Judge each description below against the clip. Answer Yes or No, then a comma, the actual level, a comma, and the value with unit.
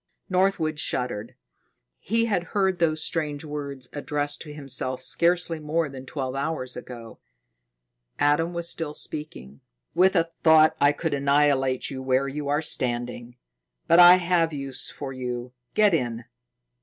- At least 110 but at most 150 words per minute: Yes, average, 145 wpm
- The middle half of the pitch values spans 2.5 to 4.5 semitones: Yes, average, 4.1 semitones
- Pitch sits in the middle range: Yes, medium, 145 Hz